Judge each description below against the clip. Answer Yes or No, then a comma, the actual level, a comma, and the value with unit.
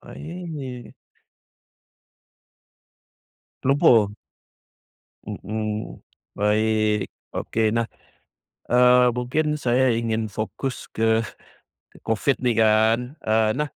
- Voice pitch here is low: Yes, low, 115 Hz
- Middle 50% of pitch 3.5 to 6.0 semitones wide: No, average, 2.8 semitones